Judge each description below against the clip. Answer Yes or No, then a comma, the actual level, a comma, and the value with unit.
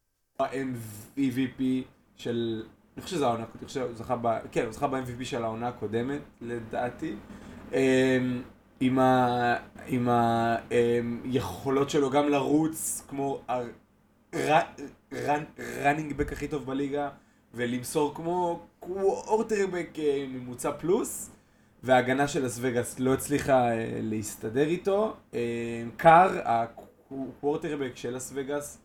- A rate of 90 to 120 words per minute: Yes, slow, 100 wpm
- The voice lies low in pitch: Yes, low, 130 Hz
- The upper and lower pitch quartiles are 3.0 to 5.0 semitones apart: Yes, average, 3.4 semitones